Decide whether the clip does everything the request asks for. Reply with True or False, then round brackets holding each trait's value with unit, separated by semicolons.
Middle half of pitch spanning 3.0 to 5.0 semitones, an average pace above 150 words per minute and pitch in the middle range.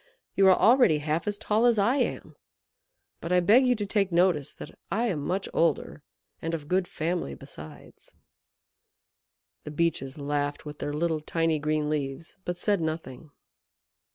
True (4.6 semitones; 160 wpm; 165 Hz)